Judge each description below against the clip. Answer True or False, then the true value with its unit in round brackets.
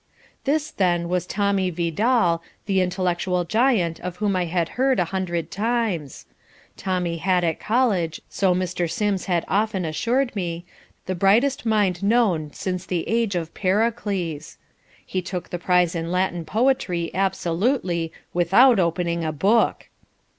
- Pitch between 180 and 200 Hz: True (185 Hz)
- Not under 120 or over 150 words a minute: True (140 wpm)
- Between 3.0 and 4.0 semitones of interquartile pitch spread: True (3.6 semitones)